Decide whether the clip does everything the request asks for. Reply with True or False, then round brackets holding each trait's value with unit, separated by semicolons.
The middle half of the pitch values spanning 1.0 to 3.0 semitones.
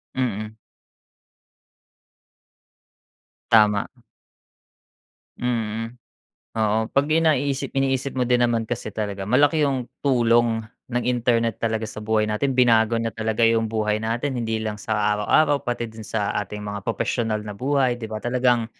True (2.5 semitones)